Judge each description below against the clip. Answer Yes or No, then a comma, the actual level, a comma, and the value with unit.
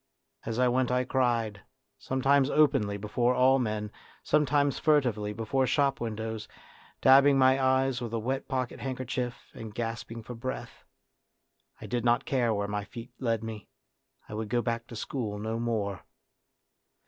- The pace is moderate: Yes, average, 155 wpm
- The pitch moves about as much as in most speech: Yes, average, 3.0 semitones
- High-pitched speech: No, low, 120 Hz